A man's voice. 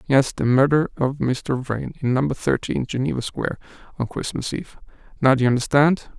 Yes: male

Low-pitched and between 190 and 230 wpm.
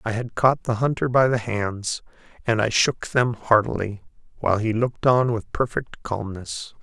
No: low, 115 Hz; average, 175 wpm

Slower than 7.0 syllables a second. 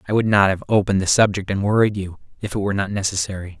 No: 7.2 syllables/s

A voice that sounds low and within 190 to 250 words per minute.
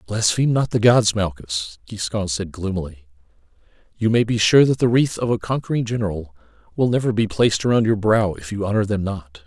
Yes: low, 105 Hz; average, 195 wpm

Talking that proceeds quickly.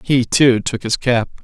Yes: fast, 210 wpm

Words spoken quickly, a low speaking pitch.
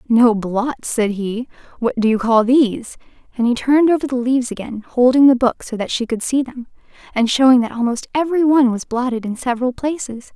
No: fast, 210 wpm; high, 245 Hz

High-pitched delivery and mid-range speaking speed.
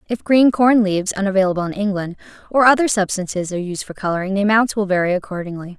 Yes: high, 200 Hz; average, 195 wpm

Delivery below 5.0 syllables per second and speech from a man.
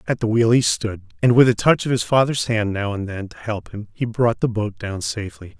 No: 5.3 syllables/s; male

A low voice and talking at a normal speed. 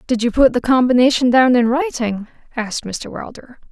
No: very high, 250 Hz; average, 180 wpm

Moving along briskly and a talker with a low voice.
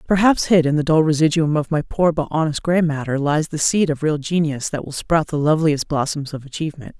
No: fast, 230 wpm; medium, 155 Hz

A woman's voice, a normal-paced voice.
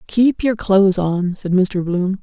Yes: female; average, 190 wpm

